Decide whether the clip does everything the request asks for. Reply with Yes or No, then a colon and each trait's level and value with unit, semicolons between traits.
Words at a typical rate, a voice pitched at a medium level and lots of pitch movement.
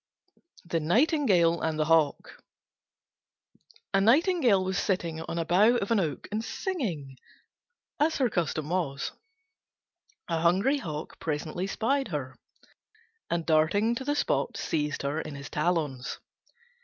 No: slow, 130 wpm; medium, 170 Hz; wide, 6.6 semitones